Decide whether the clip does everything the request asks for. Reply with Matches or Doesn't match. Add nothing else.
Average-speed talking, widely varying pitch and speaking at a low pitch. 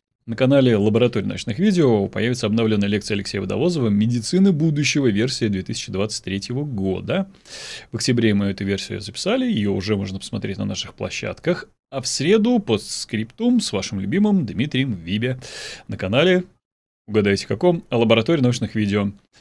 Matches